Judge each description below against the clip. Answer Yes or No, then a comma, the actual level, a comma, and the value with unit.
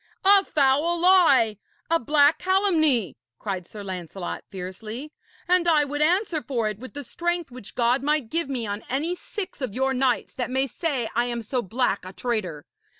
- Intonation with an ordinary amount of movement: No, wide, 6.5 semitones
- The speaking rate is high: No, average, 180 wpm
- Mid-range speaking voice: No, very high, 265 Hz